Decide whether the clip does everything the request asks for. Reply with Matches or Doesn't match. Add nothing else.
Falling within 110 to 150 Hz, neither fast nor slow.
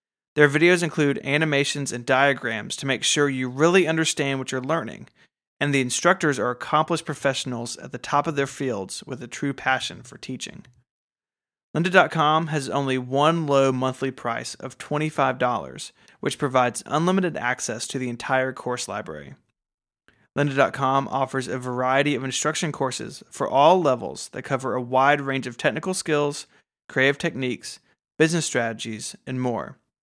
Matches